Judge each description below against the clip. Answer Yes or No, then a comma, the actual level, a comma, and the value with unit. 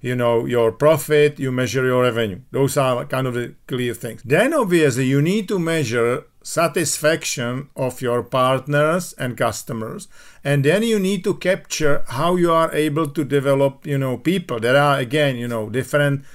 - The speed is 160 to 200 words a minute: Yes, average, 175 wpm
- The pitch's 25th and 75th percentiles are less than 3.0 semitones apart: No, average, 3.8 semitones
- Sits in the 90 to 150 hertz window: Yes, medium, 140 Hz